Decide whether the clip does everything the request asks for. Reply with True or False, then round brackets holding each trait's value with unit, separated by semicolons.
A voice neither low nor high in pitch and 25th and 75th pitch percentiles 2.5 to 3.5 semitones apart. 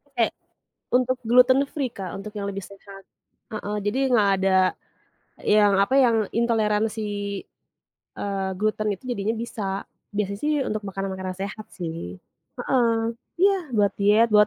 False (210 Hz; 2.8 semitones)